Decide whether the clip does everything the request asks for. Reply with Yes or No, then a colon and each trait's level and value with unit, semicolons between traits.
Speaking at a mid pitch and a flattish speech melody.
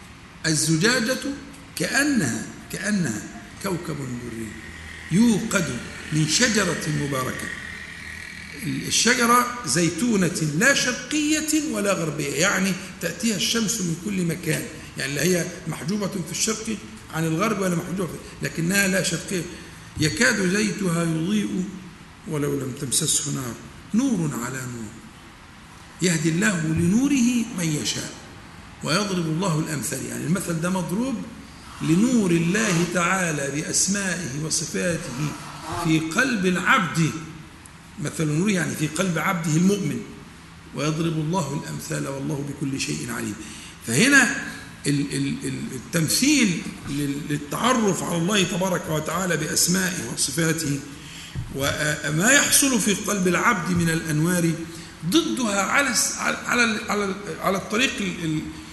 No: medium, 170 Hz; average, 4.8 semitones